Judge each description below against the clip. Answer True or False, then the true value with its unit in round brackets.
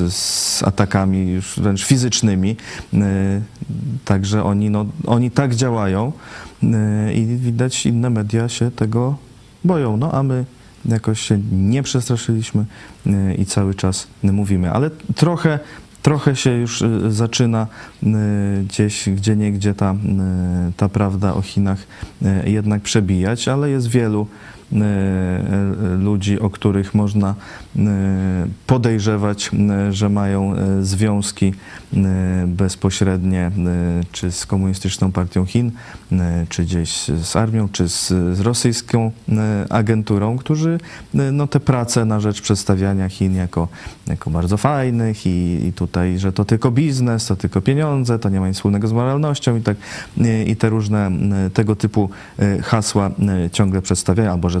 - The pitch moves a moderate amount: True (3.2 semitones)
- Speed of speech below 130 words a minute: True (120 wpm)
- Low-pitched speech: True (105 Hz)